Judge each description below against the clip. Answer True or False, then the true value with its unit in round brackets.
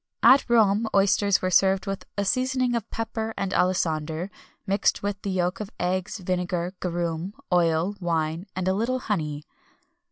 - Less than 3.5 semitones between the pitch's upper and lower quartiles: True (3.0 semitones)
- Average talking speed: True (155 wpm)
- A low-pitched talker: False (190 Hz)